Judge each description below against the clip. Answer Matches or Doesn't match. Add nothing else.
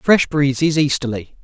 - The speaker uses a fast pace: Doesn't match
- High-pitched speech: Doesn't match